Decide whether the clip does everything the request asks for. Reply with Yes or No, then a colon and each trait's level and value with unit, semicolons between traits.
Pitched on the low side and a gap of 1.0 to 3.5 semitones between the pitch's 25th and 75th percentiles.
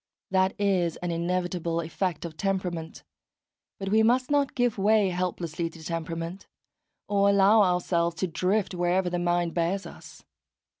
No: medium, 180 Hz; narrow, 2.6 semitones